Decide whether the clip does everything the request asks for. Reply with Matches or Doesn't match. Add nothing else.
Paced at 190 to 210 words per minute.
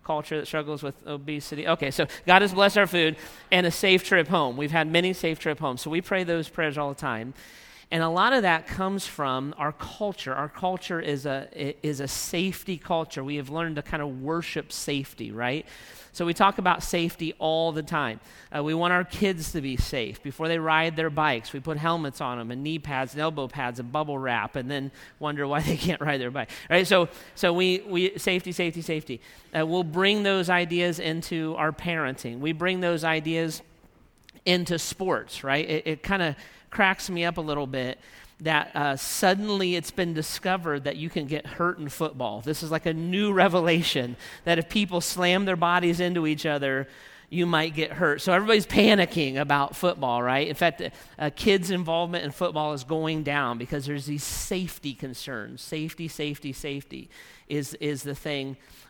Matches